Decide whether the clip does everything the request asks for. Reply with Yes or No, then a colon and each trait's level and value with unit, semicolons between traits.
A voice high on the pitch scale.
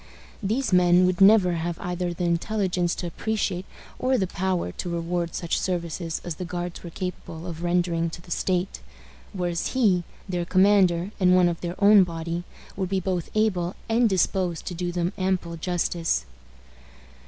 No: medium, 180 Hz